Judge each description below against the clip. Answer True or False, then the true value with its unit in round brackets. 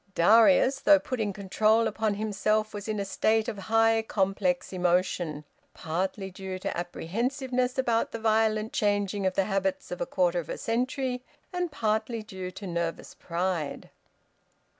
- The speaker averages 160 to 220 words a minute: False (150 wpm)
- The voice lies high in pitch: True (210 Hz)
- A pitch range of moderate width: True (3.3 semitones)